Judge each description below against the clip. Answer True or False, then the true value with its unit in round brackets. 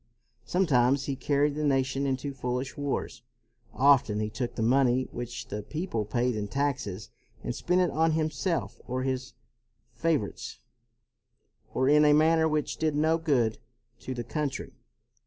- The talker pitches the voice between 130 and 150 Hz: True (135 Hz)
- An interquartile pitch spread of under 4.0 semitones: True (3.6 semitones)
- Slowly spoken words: False (150 wpm)